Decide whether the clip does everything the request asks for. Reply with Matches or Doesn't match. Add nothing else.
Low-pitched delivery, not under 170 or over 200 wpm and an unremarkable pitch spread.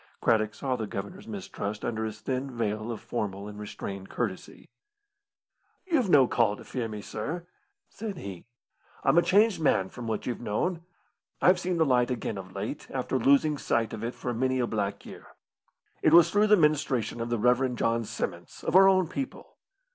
Doesn't match